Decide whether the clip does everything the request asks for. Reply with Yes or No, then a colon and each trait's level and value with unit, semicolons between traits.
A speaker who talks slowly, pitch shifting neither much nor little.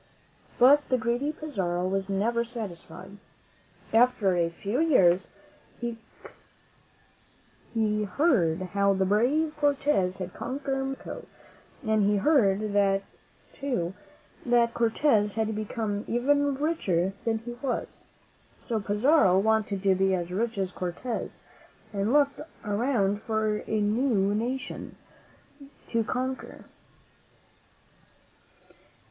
Yes: slow, 105 wpm; average, 4.6 semitones